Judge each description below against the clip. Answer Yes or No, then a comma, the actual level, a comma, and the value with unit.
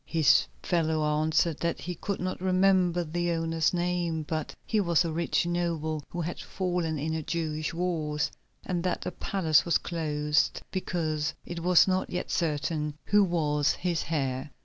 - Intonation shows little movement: Yes, narrow, 2.3 semitones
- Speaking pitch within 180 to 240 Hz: No, medium, 165 Hz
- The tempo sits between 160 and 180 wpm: Yes, average, 165 wpm